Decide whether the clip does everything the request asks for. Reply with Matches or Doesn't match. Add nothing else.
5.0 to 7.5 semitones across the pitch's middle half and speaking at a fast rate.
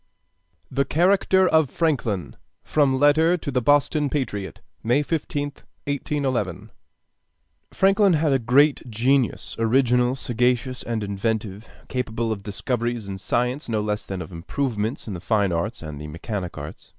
Doesn't match